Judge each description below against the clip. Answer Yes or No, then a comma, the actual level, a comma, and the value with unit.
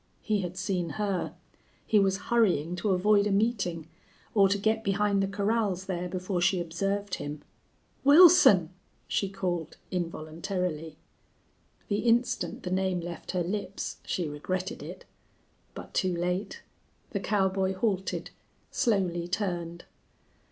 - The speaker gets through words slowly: Yes, slow, 130 wpm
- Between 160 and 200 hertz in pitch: Yes, high, 190 Hz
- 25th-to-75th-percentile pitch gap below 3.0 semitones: Yes, narrow, 2.6 semitones